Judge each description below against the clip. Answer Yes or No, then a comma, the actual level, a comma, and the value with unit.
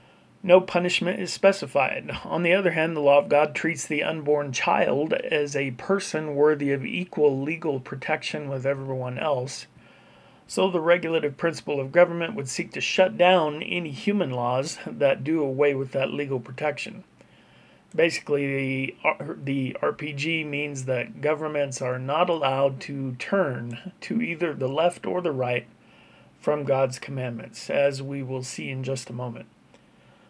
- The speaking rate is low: No, average, 155 wpm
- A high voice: No, medium, 145 Hz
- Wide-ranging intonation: No, average, 3.8 semitones